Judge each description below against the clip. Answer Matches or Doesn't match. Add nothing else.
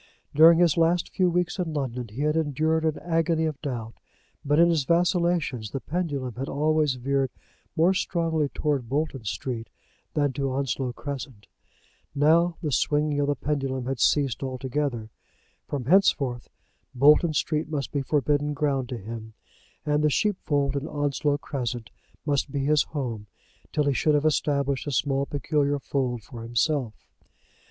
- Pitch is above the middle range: Doesn't match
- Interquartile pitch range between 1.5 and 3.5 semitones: Matches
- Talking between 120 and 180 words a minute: Matches